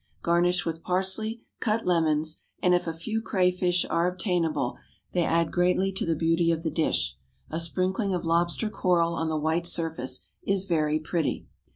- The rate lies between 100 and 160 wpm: No, average, 170 wpm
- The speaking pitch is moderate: Yes, medium, 170 Hz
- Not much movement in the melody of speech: Yes, narrow, 2.1 semitones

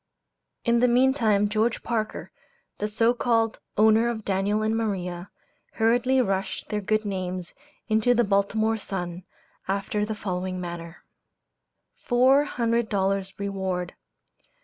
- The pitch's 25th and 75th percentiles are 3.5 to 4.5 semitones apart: No, average, 3.1 semitones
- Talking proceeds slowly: Yes, slow, 125 wpm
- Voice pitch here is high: Yes, high, 210 Hz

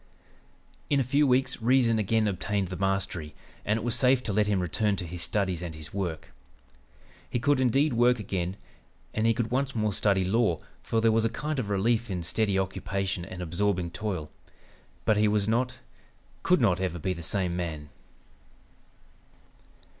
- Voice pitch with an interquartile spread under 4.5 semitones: Yes, average, 4.1 semitones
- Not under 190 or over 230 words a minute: No, average, 175 wpm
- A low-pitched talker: Yes, low, 105 Hz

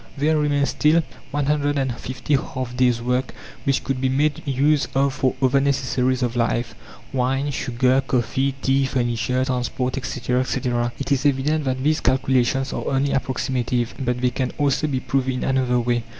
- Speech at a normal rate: Yes, average, 165 wpm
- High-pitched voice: No, low, 130 Hz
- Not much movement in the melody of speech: Yes, narrow, 1.8 semitones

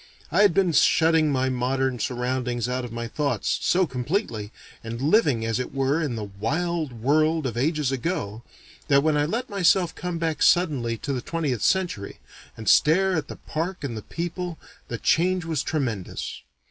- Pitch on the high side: No, medium, 145 Hz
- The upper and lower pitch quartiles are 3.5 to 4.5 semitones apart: No, wide, 5.4 semitones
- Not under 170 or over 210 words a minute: Yes, average, 175 wpm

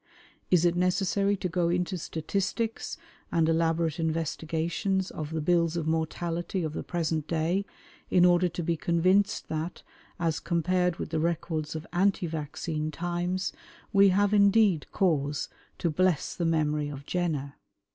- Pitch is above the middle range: No, medium, 170 Hz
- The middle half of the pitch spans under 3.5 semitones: Yes, narrow, 2.4 semitones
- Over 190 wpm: No, average, 145 wpm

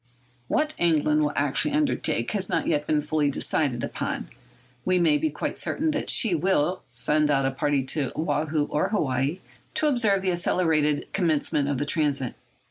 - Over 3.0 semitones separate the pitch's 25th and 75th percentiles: Yes, average, 4.0 semitones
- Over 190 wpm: No, average, 170 wpm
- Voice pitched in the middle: Yes, medium, 155 Hz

